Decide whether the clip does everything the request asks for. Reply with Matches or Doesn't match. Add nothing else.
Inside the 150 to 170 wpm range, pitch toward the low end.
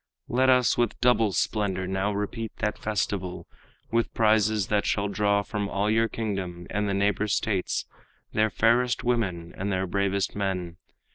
Matches